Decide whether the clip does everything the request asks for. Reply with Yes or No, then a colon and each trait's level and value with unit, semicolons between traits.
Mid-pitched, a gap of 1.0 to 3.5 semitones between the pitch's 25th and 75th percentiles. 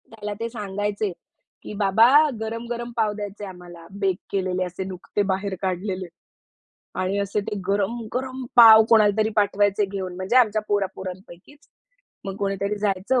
No: high, 205 Hz; narrow, 2.4 semitones